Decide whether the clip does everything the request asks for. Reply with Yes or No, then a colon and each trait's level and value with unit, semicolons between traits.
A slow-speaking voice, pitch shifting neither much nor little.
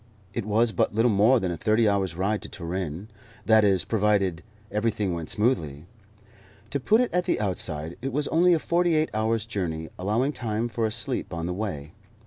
No: average, 195 wpm; average, 4.4 semitones